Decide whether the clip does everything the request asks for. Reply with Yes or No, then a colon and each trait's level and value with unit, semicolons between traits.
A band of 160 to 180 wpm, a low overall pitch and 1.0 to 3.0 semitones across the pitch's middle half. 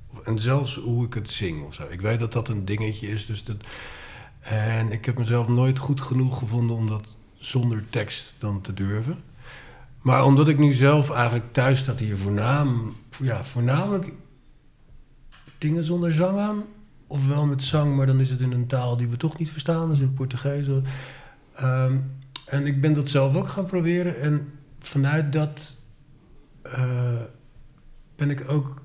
No: average, 175 wpm; low, 130 Hz; average, 3.4 semitones